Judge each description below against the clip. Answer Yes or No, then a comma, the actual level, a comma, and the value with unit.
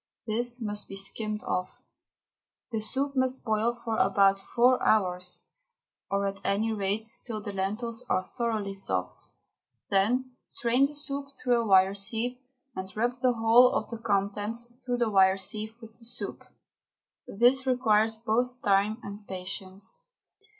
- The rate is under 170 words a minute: Yes, average, 150 wpm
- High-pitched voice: Yes, high, 220 Hz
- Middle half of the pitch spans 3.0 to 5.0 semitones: Yes, average, 3.6 semitones